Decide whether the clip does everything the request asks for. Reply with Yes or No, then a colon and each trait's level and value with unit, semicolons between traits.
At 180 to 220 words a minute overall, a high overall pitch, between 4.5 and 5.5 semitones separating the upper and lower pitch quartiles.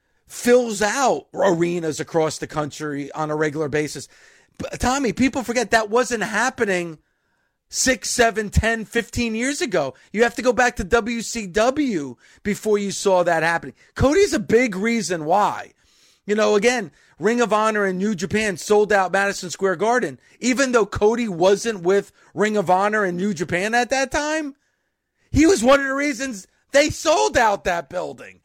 No: average, 165 wpm; high, 215 Hz; average, 5.1 semitones